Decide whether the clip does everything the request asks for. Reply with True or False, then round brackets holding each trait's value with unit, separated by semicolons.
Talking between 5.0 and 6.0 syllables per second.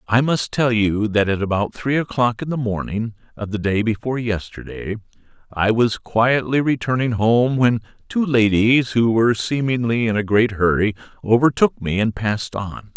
False (4.8 syllables/s)